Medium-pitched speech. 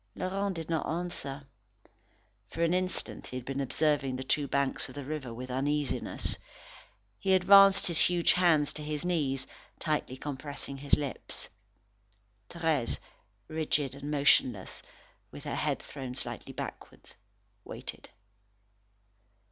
Yes: medium, 150 Hz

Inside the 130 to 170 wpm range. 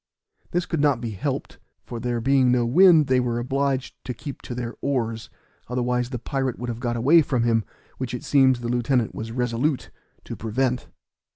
No: average, 190 wpm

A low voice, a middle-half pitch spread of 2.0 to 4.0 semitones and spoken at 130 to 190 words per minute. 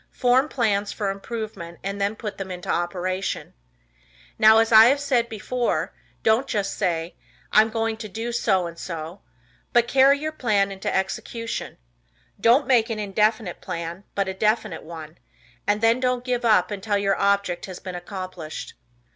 No: high, 205 Hz; average, 3.7 semitones; average, 165 wpm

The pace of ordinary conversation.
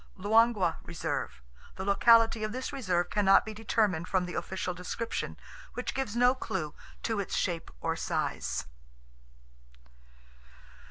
No: slow, 120 wpm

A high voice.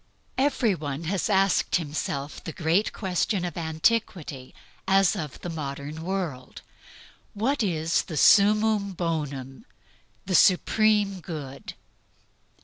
No: medium, 175 Hz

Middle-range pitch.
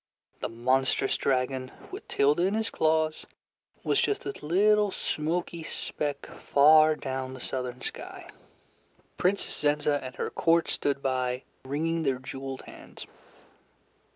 Yes: medium, 145 Hz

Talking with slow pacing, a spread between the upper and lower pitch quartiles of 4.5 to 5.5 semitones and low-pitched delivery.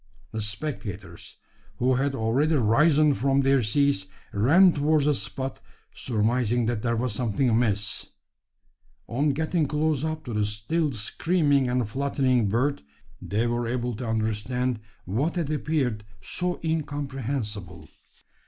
Yes: slow, 130 wpm; average, 4.8 semitones; low, 125 Hz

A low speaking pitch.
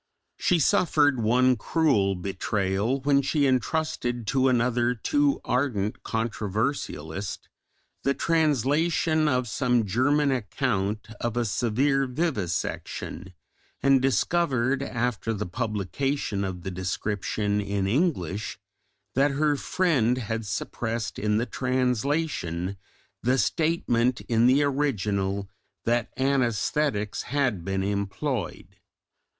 Yes: low, 120 Hz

